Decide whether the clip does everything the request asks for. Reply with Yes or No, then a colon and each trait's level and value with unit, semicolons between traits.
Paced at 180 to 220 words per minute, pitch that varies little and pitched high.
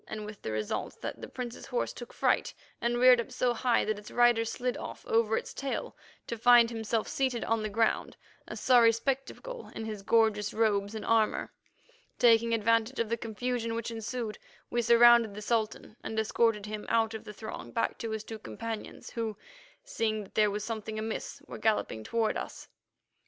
Yes: average, 185 wpm; narrow, 1.6 semitones; high, 225 Hz